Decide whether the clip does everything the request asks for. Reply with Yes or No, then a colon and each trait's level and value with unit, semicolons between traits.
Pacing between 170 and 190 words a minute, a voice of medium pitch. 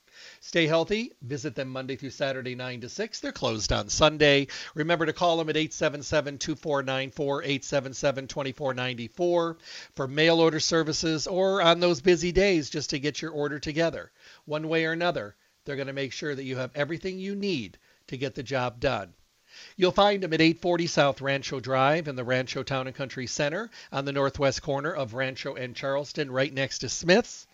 Yes: average, 185 wpm; medium, 145 Hz